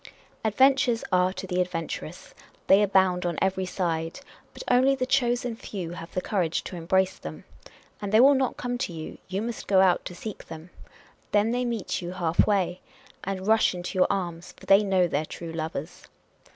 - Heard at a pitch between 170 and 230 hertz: Yes, high, 190 Hz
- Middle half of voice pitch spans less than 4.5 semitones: Yes, average, 4.0 semitones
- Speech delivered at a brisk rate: No, average, 185 wpm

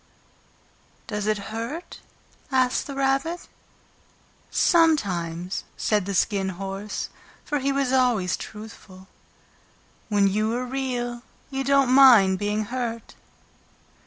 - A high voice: Yes, high, 230 Hz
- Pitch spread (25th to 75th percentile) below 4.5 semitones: No, average, 5.1 semitones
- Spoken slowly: Yes, slow, 105 wpm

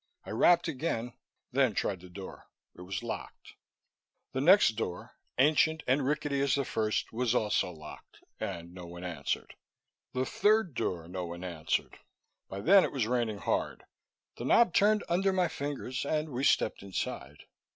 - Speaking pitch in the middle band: No, low, 125 Hz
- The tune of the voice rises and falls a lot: Yes, wide, 8.7 semitones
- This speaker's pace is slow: No, average, 160 wpm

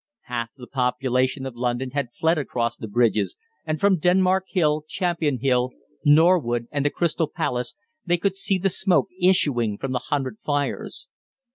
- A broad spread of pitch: Yes, wide, 5.8 semitones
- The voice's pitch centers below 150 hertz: Yes, medium, 140 Hz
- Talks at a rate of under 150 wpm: No, average, 160 wpm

